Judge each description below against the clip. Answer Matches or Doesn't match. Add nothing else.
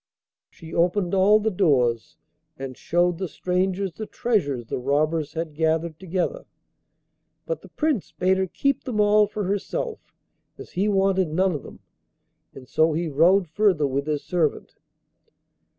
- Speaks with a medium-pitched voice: Matches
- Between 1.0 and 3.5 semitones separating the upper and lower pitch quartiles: Doesn't match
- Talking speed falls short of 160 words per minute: Matches